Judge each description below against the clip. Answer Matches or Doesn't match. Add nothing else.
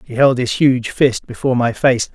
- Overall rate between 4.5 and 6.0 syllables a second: Matches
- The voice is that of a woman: Doesn't match